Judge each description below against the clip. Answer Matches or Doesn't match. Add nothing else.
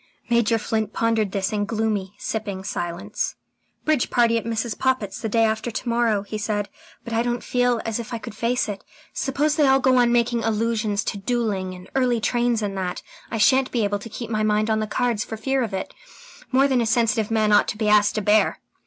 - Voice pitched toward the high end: Matches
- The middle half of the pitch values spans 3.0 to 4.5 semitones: Doesn't match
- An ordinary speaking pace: Doesn't match